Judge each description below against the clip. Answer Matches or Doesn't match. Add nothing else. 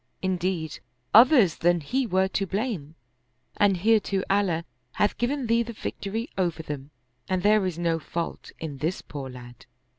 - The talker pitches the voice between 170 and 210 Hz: Matches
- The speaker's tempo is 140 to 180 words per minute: Matches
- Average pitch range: Matches